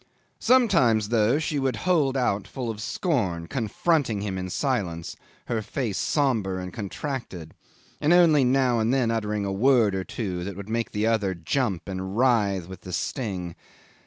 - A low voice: Yes, low, 110 Hz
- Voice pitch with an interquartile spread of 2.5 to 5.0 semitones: No, wide, 5.6 semitones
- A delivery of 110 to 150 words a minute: No, average, 165 wpm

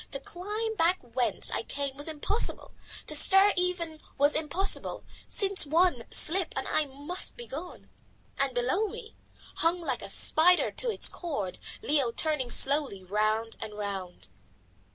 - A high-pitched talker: Yes, very high, 305 Hz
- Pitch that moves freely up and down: Yes, wide, 6.4 semitones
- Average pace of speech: Yes, average, 150 wpm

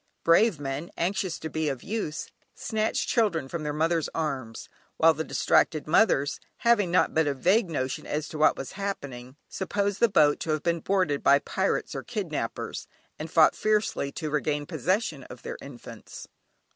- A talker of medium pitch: Yes, medium, 160 Hz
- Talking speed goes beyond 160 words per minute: Yes, average, 170 wpm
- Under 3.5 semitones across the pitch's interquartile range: No, average, 4.7 semitones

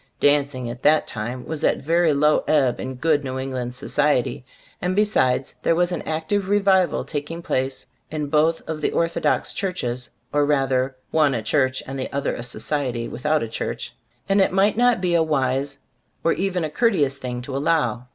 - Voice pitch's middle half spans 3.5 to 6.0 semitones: Yes, average, 4.3 semitones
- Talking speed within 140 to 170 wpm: No, average, 195 wpm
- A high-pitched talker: No, medium, 145 Hz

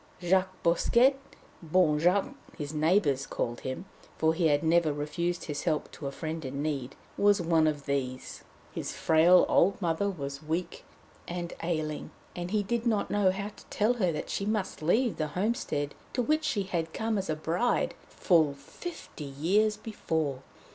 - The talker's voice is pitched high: No, medium, 170 Hz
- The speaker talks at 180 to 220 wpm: No, average, 170 wpm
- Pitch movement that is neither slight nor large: Yes, average, 4.9 semitones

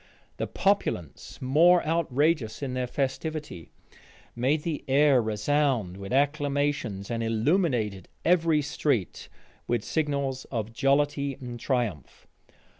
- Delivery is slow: Yes, slow, 110 wpm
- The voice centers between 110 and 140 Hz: Yes, low, 135 Hz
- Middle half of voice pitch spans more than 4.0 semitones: Yes, average, 4.4 semitones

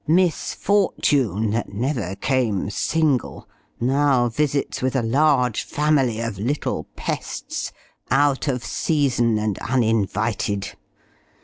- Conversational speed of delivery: No, slow, 105 wpm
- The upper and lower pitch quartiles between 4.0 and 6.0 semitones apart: Yes, average, 4.5 semitones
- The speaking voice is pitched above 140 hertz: No, low, 125 Hz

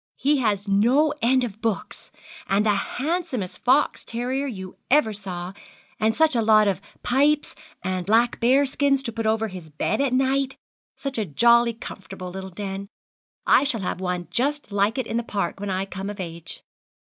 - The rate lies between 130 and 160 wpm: No, average, 180 wpm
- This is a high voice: Yes, high, 220 Hz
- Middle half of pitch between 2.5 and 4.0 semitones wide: No, average, 5.2 semitones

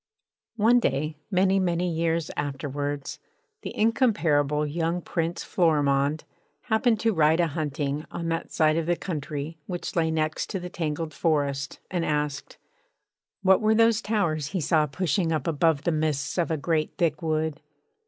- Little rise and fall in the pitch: No, average, 3.1 semitones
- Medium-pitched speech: Yes, medium, 160 Hz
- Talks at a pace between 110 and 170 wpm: Yes, average, 155 wpm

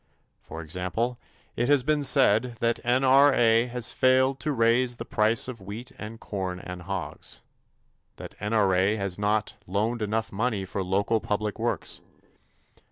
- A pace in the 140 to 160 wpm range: Yes, average, 145 wpm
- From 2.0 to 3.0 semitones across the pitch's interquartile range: No, average, 3.9 semitones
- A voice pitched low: Yes, low, 110 Hz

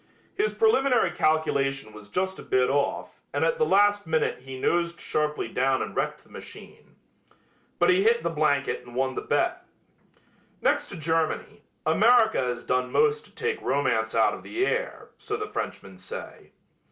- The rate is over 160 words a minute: Yes, average, 170 wpm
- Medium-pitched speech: Yes, medium, 165 Hz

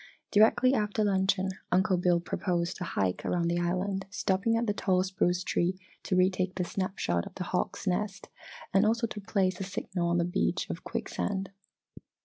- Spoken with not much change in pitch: Yes, narrow, 2.1 semitones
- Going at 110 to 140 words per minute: No, average, 180 wpm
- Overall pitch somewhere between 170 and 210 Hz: Yes, high, 190 Hz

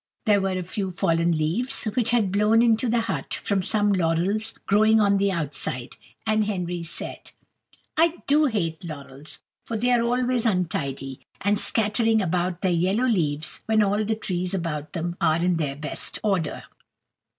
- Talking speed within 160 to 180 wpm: Yes, average, 165 wpm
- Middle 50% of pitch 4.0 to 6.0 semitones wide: Yes, average, 4.7 semitones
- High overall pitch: Yes, high, 195 Hz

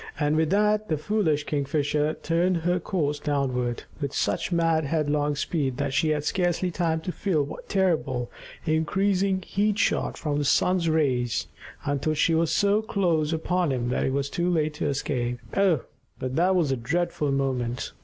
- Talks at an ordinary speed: Yes, average, 175 wpm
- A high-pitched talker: No, medium, 155 Hz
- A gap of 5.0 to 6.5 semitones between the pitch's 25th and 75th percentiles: No, average, 3.8 semitones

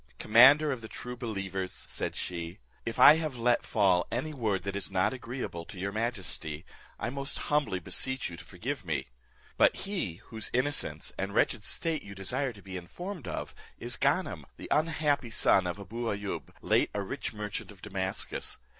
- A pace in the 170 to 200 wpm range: Yes, average, 180 wpm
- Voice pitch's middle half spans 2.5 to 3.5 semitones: No, wide, 5.4 semitones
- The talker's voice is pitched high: No, low, 110 Hz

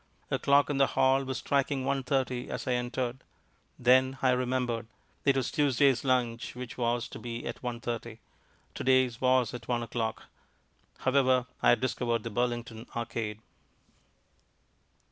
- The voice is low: Yes, low, 125 Hz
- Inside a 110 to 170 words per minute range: Yes, average, 155 wpm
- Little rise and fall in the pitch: Yes, narrow, 1.9 semitones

